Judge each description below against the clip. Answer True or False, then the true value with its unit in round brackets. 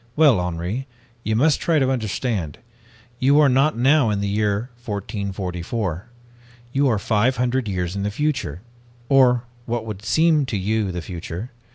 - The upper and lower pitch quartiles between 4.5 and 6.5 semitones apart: True (5.0 semitones)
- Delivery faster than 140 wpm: True (160 wpm)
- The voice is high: False (110 Hz)